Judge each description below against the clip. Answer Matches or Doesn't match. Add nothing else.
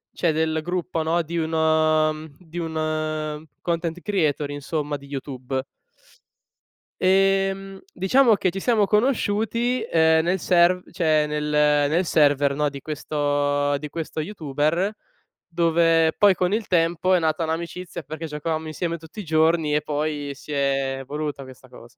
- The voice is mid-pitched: Matches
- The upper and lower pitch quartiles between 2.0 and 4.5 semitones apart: Matches